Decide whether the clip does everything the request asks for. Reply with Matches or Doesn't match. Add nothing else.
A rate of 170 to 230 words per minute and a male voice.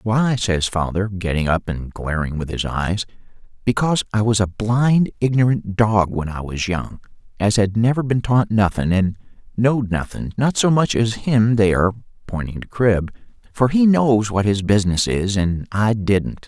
Matches